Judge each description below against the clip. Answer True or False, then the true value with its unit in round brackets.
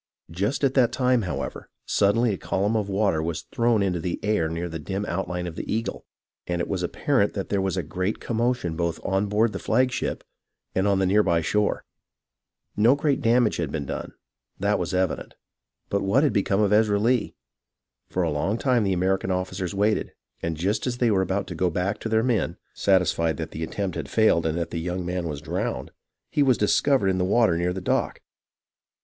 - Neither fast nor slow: False (210 wpm)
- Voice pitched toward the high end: False (95 Hz)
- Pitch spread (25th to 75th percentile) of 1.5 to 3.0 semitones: False (3.8 semitones)